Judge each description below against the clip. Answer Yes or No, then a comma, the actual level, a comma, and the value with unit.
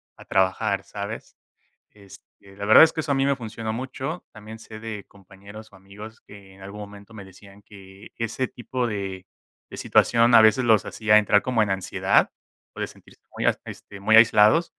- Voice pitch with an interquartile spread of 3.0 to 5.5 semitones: No, narrow, 2.4 semitones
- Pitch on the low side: Yes, low, 105 Hz